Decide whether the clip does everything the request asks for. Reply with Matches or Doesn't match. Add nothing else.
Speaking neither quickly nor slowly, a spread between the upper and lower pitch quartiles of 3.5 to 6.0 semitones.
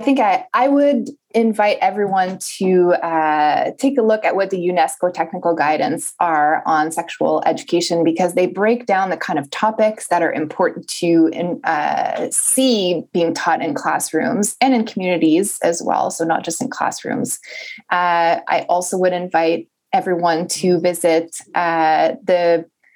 Matches